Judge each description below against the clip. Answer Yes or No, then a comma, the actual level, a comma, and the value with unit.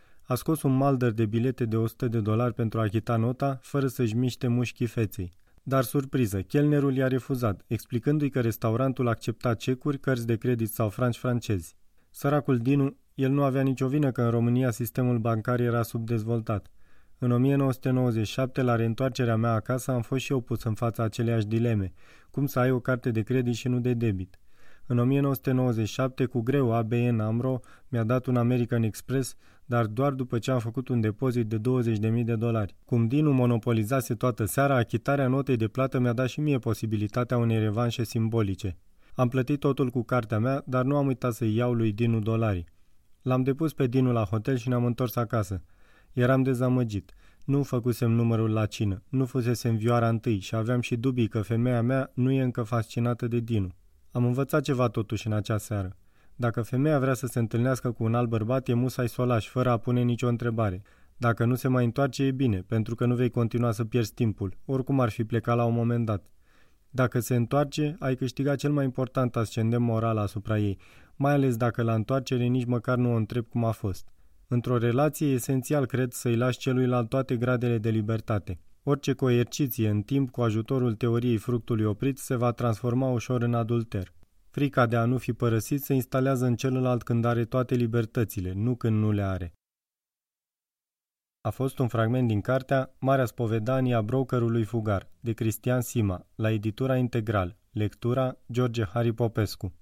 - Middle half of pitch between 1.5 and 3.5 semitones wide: Yes, narrow, 2.4 semitones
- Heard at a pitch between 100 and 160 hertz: Yes, low, 120 Hz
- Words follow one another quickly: Yes, fast, 185 wpm